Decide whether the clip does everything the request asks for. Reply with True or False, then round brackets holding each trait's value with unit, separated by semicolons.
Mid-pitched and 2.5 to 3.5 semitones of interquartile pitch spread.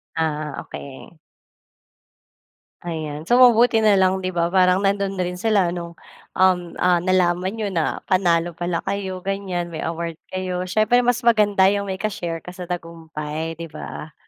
True (180 Hz; 2.8 semitones)